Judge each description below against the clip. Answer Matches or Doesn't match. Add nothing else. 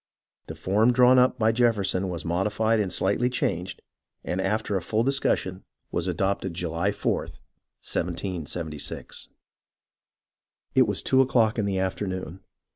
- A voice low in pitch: Matches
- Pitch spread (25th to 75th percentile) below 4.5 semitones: Matches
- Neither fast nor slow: Doesn't match